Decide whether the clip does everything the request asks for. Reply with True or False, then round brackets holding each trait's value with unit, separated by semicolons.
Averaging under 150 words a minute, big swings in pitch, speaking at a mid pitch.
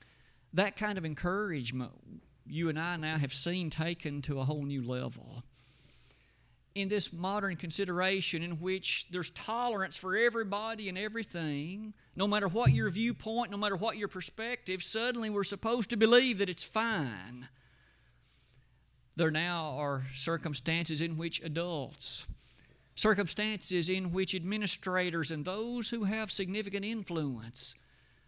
True (135 wpm; 5.9 semitones; 180 Hz)